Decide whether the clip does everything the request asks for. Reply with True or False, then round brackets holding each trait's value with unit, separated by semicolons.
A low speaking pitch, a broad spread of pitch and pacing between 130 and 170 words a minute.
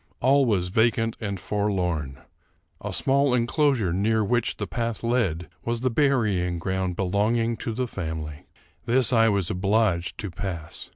False (105 Hz; 4.7 semitones; 150 wpm)